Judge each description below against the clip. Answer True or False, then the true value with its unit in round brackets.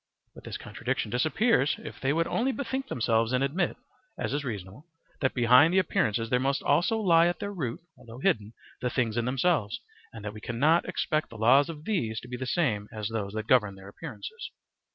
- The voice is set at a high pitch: False (130 Hz)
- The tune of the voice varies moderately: False (6.8 semitones)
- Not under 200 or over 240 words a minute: True (205 wpm)